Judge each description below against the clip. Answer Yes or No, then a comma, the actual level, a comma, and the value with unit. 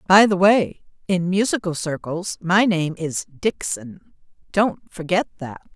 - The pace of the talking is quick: No, slow, 135 wpm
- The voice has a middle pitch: Yes, medium, 180 Hz